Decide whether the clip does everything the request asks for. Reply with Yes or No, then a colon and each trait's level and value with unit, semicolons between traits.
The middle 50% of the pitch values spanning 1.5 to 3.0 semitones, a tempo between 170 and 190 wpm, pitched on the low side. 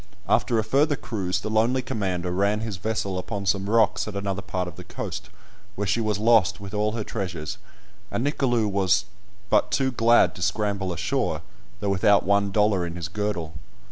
Yes: average, 2.7 semitones; average, 185 wpm; low, 100 Hz